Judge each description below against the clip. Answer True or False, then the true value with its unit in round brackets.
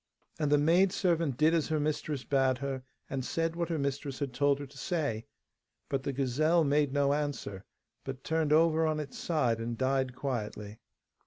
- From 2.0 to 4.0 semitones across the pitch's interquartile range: True (3.0 semitones)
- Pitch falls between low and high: True (145 Hz)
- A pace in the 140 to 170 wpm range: False (180 wpm)